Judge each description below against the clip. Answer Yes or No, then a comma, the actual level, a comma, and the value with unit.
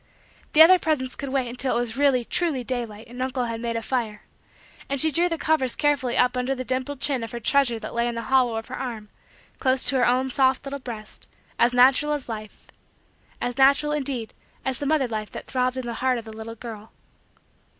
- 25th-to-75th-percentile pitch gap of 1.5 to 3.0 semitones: Yes, narrow, 2.6 semitones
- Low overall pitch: No, very high, 255 Hz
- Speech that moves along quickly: Yes, fast, 225 wpm